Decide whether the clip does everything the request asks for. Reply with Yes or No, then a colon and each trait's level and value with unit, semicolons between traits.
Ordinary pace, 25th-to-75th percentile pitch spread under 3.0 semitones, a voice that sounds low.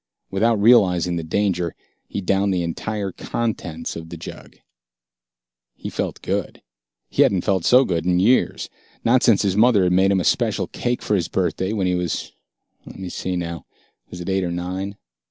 Yes: average, 185 wpm; narrow, 2.6 semitones; very low, 95 Hz